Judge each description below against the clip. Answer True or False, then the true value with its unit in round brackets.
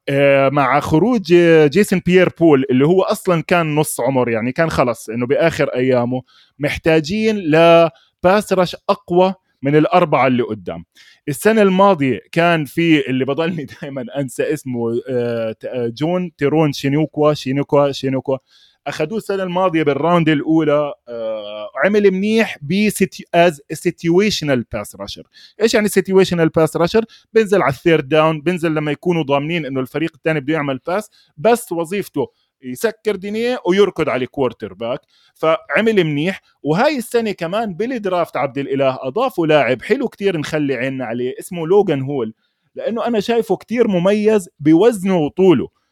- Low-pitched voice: False (160 Hz)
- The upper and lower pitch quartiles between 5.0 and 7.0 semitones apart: True (5.4 semitones)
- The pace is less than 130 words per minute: False (135 wpm)